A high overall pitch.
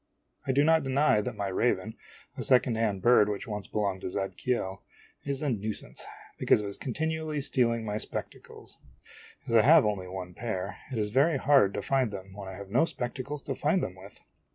No: low, 110 Hz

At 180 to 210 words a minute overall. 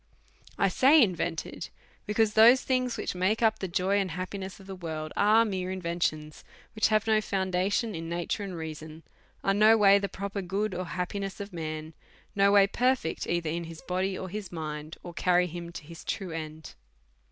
Yes: average, 200 wpm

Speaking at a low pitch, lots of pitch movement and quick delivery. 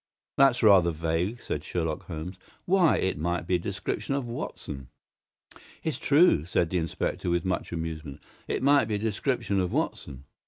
No: very low, 90 Hz; wide, 6.3 semitones; average, 165 wpm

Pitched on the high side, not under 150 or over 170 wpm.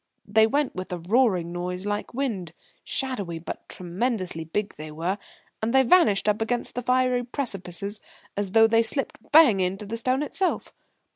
Yes: high, 210 Hz; average, 165 wpm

